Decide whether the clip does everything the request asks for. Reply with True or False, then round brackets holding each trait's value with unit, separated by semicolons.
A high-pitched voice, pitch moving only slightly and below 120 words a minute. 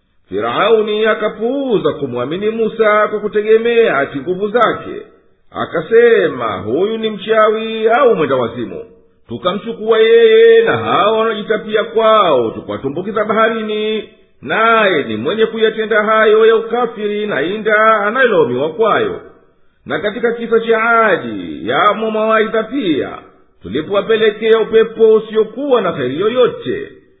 True (220 Hz; 1.3 semitones; 105 wpm)